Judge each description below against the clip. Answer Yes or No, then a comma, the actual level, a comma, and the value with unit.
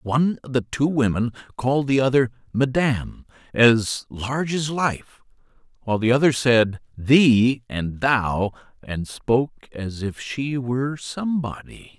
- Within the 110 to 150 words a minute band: Yes, slow, 135 wpm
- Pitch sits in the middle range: No, low, 125 Hz